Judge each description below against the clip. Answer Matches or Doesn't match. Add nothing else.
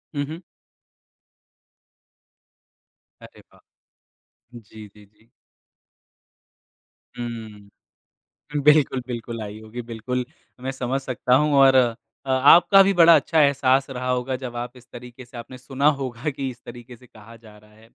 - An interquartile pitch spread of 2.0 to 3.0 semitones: Matches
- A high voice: Doesn't match